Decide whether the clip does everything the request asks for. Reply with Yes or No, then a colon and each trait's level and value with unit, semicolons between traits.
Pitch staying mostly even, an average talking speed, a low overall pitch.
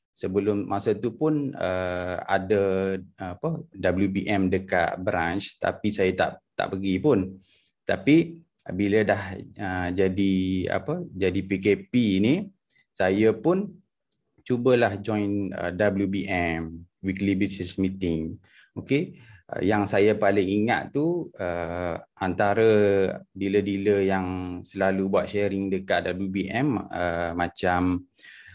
Yes: narrow, 2.1 semitones; average, 110 wpm; very low, 95 Hz